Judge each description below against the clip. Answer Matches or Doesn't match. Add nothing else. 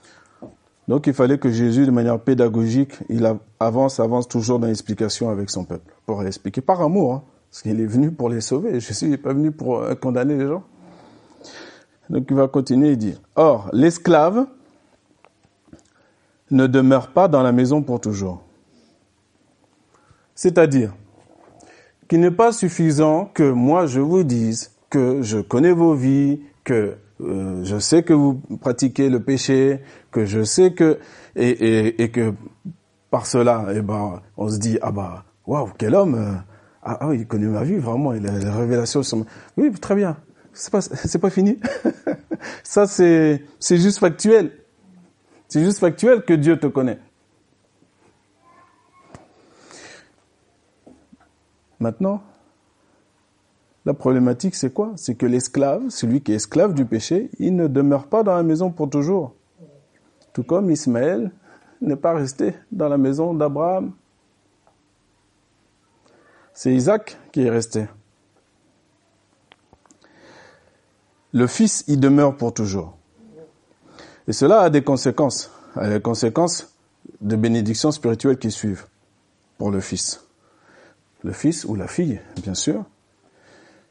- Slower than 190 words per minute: Matches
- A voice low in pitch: Matches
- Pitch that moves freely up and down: Matches